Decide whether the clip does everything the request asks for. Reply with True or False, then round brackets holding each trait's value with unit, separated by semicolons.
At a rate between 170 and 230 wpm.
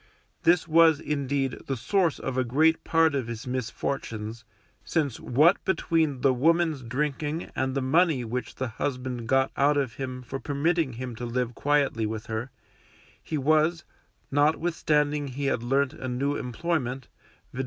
False (155 wpm)